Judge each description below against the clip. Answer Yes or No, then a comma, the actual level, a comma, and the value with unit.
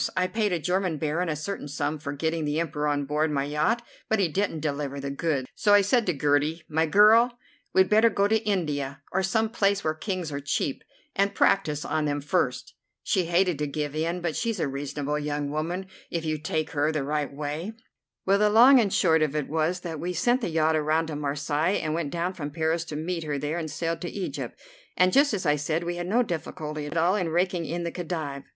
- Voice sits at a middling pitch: Yes, medium, 160 Hz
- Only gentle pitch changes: No, average, 3.8 semitones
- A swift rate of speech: Yes, fast, 230 wpm